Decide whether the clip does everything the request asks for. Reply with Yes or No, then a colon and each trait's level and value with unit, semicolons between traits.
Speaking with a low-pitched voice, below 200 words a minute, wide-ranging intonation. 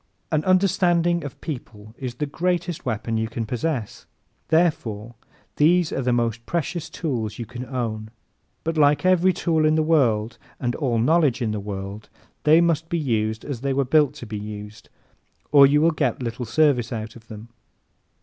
Yes: low, 130 Hz; average, 180 wpm; wide, 6.1 semitones